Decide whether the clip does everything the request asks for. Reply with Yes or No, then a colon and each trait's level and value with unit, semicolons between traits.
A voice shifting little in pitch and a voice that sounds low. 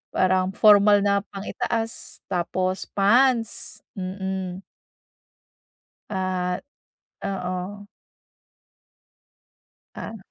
No: narrow, 1.8 semitones; high, 190 Hz